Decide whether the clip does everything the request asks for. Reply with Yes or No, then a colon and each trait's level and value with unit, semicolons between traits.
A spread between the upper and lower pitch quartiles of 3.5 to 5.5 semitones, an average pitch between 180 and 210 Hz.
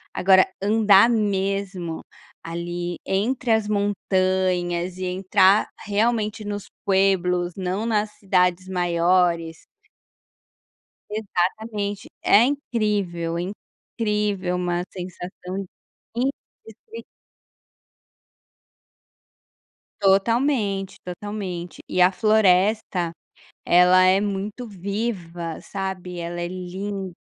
No: average, 2.7 semitones; high, 190 Hz